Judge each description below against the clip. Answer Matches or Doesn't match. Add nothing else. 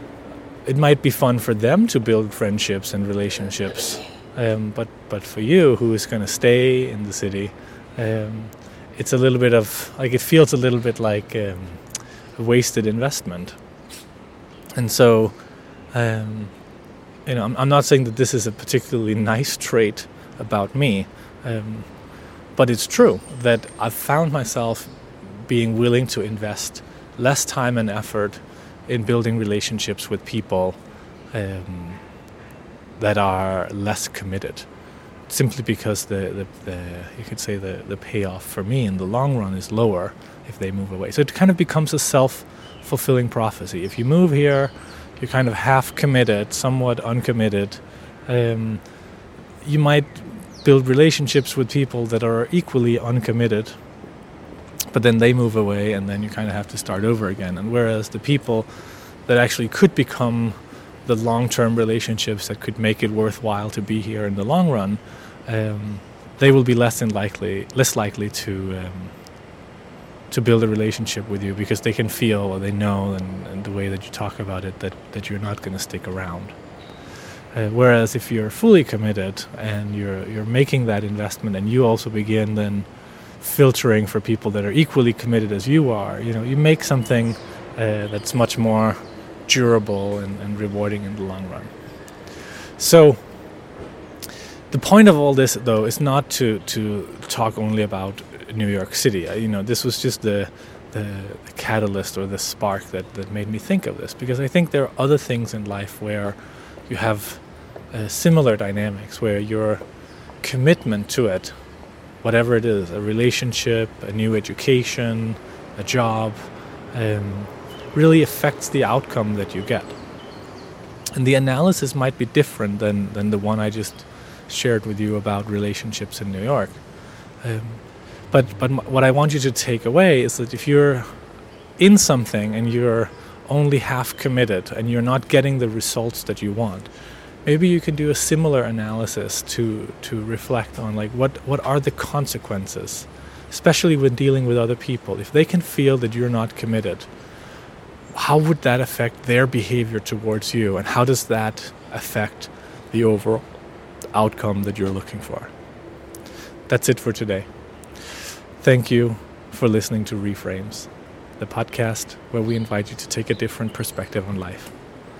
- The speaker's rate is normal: Matches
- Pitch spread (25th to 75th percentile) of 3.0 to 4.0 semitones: Matches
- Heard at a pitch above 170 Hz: Doesn't match